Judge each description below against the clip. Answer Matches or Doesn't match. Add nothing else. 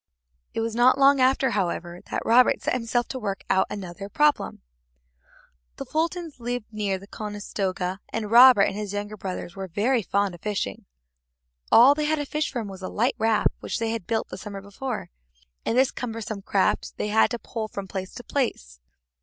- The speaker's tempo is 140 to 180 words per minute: Doesn't match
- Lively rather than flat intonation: Doesn't match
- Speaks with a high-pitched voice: Matches